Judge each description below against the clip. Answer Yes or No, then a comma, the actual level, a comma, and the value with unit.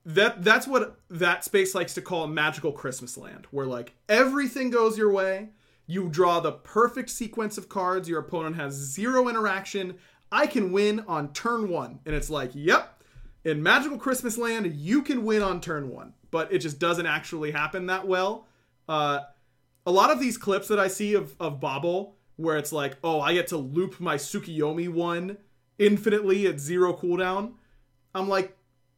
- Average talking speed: Yes, average, 180 wpm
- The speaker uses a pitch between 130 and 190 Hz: Yes, medium, 185 Hz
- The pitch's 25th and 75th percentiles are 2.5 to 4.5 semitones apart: No, average, 5.1 semitones